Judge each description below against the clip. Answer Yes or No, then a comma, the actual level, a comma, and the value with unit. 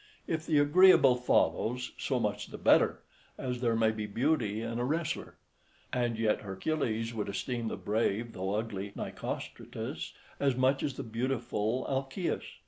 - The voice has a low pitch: Yes, low, 120 Hz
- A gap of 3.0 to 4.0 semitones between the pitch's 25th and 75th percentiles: Yes, average, 3.7 semitones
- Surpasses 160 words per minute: No, average, 150 wpm